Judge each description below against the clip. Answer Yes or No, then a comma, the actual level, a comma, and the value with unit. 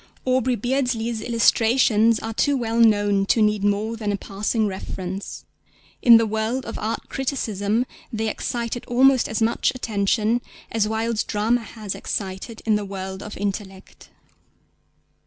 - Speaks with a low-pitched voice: No, high, 220 Hz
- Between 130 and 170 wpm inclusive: Yes, average, 140 wpm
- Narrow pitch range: Yes, narrow, 2.3 semitones